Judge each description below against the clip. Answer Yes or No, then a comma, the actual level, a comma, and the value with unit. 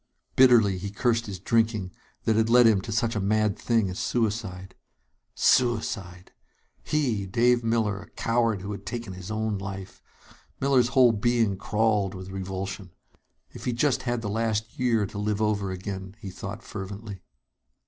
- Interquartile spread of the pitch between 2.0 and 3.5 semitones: Yes, average, 3.0 semitones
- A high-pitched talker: No, low, 105 Hz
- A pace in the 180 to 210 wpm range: No, average, 160 wpm